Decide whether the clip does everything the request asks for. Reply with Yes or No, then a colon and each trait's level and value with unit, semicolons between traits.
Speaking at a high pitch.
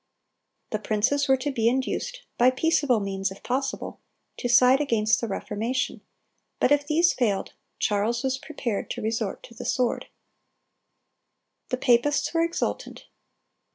Yes: very high, 250 Hz